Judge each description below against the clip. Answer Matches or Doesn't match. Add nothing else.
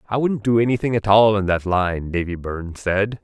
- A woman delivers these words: Doesn't match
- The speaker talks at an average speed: Doesn't match